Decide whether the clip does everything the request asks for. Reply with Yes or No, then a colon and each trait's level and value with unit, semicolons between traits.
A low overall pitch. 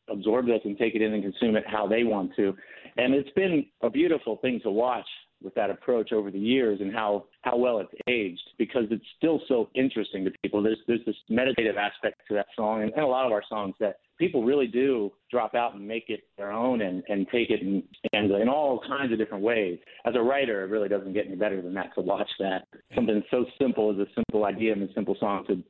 Yes: low, 110 Hz